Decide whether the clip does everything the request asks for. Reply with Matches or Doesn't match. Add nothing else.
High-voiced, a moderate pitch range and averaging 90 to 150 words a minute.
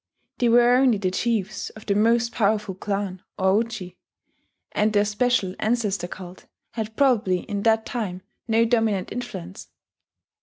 Matches